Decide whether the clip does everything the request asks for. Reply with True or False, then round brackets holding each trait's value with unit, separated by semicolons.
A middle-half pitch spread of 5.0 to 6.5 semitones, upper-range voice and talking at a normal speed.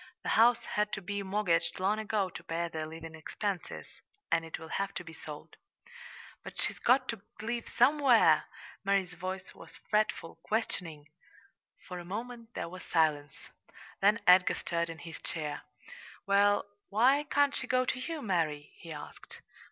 True (5.4 semitones; 195 Hz; 160 wpm)